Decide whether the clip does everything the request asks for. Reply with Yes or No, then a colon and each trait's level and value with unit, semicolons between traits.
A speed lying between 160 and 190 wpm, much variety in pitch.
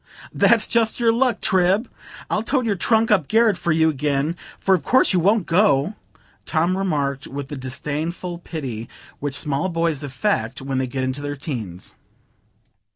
Yes: average, 165 wpm; wide, 6.3 semitones